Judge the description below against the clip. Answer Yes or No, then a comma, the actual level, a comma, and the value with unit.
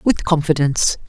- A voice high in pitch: No, medium, 155 Hz